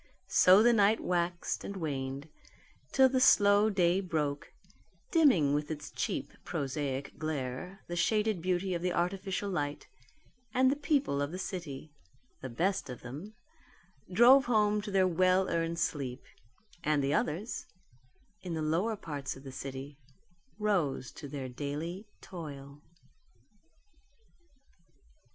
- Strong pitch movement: Yes, wide, 5.9 semitones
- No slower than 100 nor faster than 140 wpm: Yes, slow, 135 wpm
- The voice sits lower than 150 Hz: No, medium, 170 Hz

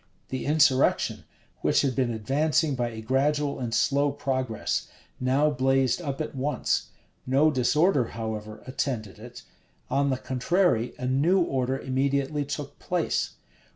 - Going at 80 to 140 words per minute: Yes, slow, 135 wpm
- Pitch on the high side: No, low, 135 Hz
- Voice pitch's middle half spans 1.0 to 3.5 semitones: Yes, narrow, 2.6 semitones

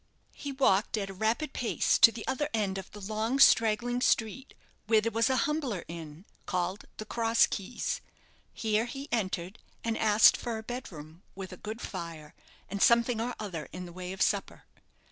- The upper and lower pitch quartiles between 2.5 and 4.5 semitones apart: Yes, average, 3.9 semitones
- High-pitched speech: Yes, high, 215 Hz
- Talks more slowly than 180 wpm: No, average, 185 wpm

